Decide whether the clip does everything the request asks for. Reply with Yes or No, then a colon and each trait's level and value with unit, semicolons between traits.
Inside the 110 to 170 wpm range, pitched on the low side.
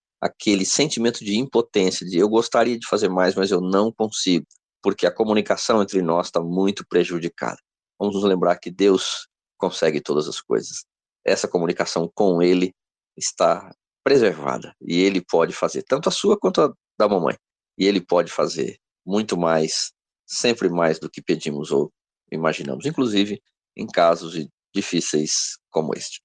Yes: average, 155 wpm; very low, 95 Hz